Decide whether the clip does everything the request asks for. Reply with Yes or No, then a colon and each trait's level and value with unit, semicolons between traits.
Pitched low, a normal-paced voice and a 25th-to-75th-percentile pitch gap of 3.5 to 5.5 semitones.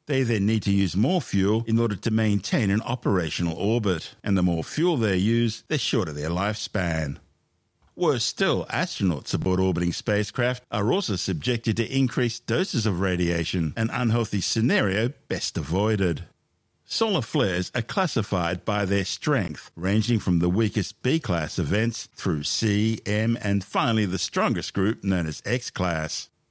Yes: low, 105 Hz; average, 155 wpm; average, 4.2 semitones